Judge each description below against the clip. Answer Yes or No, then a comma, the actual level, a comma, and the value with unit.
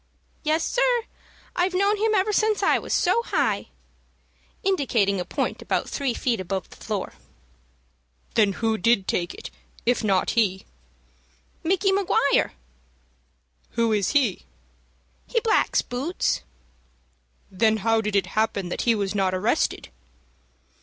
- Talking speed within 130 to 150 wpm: Yes, slow, 135 wpm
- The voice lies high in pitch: Yes, high, 230 Hz